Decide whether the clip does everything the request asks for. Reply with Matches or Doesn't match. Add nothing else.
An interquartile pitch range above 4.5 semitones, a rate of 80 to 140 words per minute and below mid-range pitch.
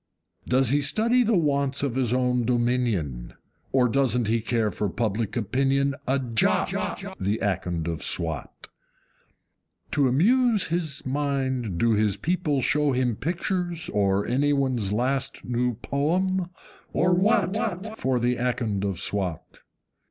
Matches